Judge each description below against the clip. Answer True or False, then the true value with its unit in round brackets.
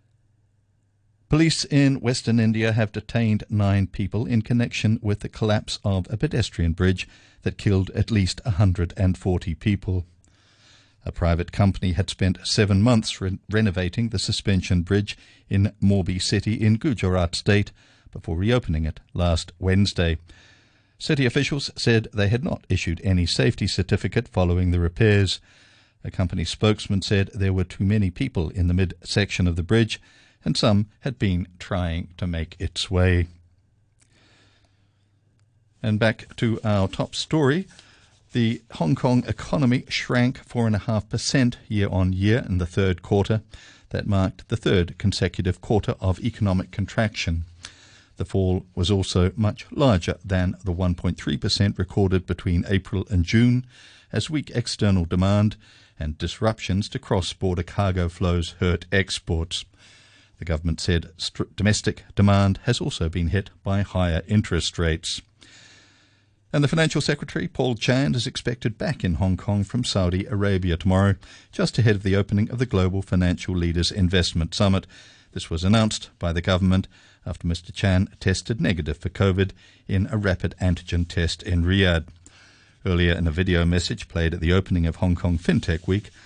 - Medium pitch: False (100 Hz)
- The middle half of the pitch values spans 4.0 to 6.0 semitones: False (3.2 semitones)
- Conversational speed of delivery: True (150 wpm)